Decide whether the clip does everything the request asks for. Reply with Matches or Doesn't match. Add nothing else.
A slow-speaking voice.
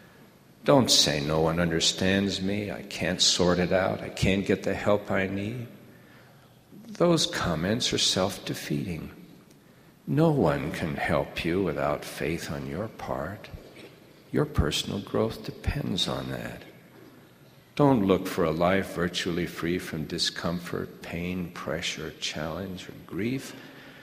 Matches